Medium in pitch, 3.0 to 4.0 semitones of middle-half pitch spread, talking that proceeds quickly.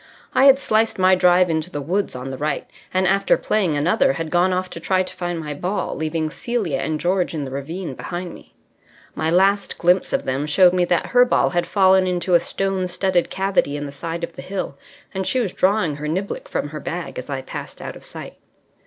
Yes: medium, 180 Hz; average, 3.4 semitones; fast, 225 wpm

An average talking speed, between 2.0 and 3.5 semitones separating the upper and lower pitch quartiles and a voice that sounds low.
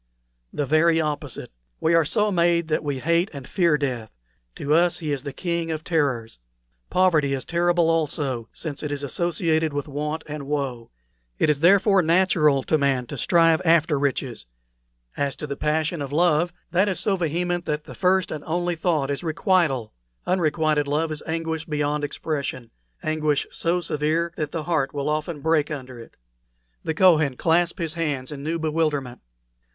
No: average, 175 wpm; average, 2.8 semitones; medium, 155 Hz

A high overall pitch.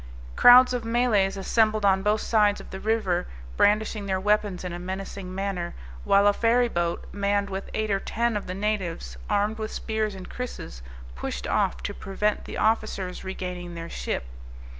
Yes: high, 200 Hz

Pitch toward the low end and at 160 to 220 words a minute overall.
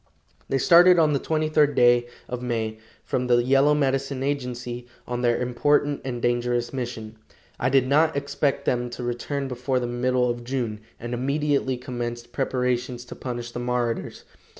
Yes: low, 125 Hz; average, 165 wpm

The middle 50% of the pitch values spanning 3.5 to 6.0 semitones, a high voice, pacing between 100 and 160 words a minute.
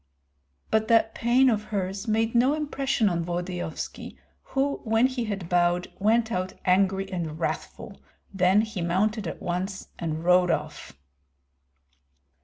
Yes: average, 4.1 semitones; high, 195 Hz; slow, 135 wpm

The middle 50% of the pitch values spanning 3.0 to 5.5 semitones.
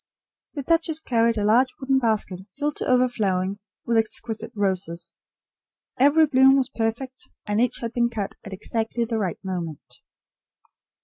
Yes: average, 4.2 semitones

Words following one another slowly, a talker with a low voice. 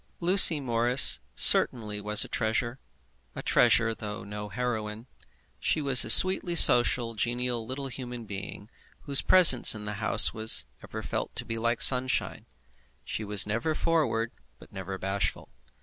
No: average, 150 wpm; low, 115 Hz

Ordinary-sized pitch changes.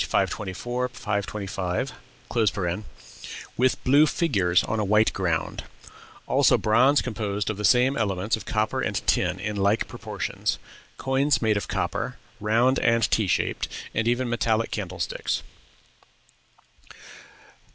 Yes: average, 3.5 semitones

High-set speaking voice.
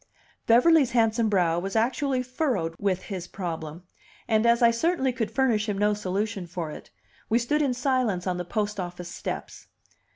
Yes: high, 215 Hz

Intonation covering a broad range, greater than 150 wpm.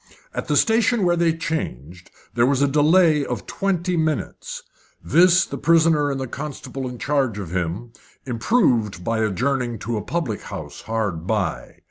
Yes: wide, 6.8 semitones; average, 160 wpm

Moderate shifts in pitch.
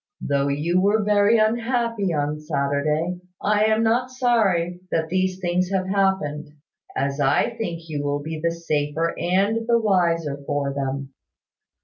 No: wide, 5.9 semitones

